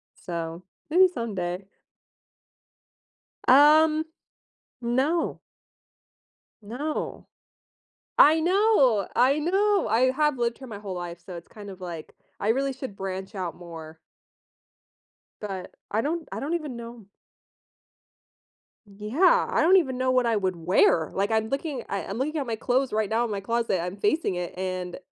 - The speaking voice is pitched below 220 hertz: No, high, 230 Hz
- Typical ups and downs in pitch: No, wide, 7.2 semitones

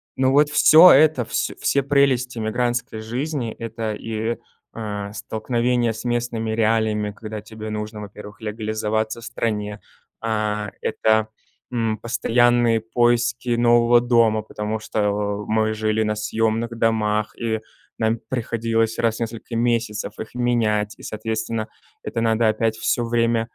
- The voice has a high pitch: No, low, 115 Hz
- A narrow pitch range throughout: Yes, narrow, 1.6 semitones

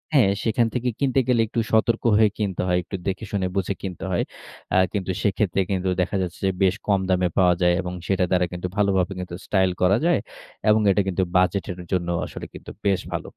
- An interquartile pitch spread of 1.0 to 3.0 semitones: Yes, narrow, 2.5 semitones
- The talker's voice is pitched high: No, very low, 95 Hz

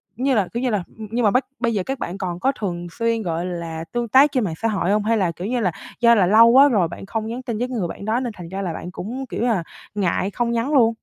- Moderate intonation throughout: Yes, average, 4.7 semitones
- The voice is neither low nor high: No, high, 220 Hz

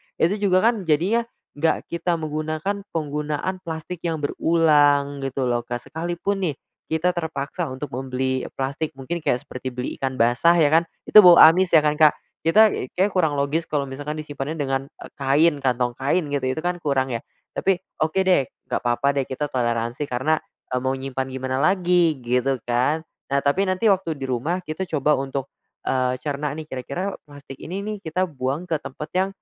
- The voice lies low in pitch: No, medium, 150 Hz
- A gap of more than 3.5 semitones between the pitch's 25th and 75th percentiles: Yes, average, 4.2 semitones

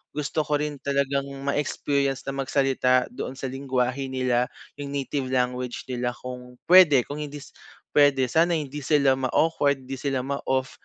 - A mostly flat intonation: Yes, narrow, 1.9 semitones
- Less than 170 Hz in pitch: Yes, low, 135 Hz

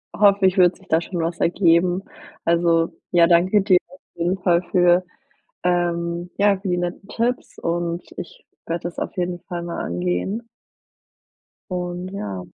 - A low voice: No, medium, 175 Hz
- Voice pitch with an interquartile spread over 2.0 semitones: No, narrow, 1.7 semitones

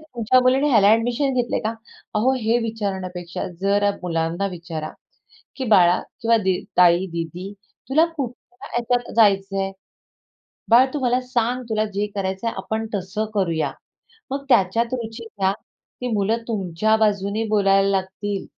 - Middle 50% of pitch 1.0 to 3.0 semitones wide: No, average, 3.7 semitones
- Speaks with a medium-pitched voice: No, high, 210 Hz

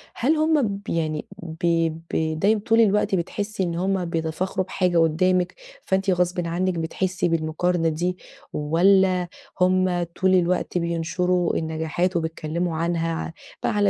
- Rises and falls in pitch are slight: Yes, narrow, 2.3 semitones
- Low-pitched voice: No, medium, 175 Hz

